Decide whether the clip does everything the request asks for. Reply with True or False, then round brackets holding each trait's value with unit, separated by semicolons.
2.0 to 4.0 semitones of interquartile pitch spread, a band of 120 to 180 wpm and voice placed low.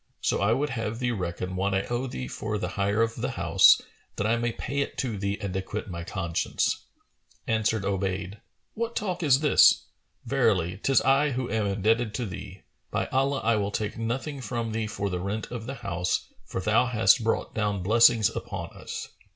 False (3.7 semitones; 195 wpm; 110 Hz)